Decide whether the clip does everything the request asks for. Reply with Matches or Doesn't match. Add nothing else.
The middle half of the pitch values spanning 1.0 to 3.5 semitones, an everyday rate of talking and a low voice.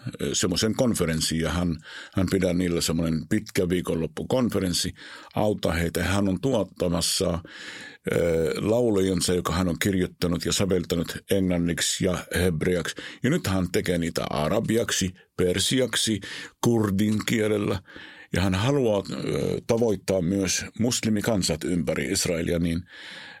Matches